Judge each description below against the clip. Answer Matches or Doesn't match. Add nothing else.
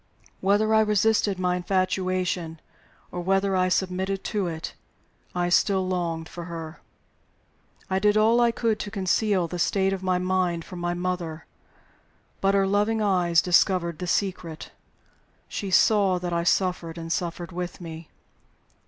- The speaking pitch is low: Doesn't match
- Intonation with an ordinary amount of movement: Doesn't match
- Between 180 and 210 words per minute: Doesn't match